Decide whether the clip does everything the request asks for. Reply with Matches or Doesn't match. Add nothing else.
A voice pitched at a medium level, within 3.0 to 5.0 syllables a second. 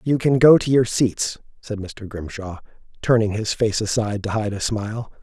Doesn't match